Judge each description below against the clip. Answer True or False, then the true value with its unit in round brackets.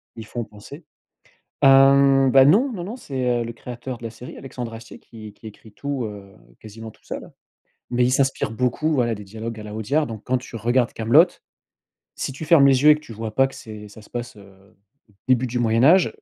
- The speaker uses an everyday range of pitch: True (3.6 semitones)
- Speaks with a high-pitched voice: False (120 Hz)